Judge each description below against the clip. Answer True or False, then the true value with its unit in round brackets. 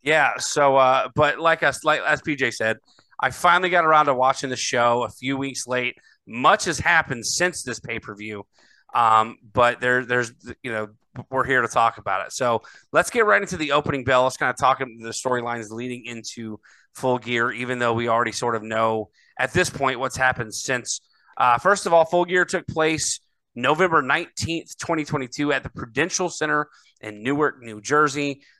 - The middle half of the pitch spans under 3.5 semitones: False (4.0 semitones)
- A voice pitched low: True (130 Hz)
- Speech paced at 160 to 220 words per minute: True (195 wpm)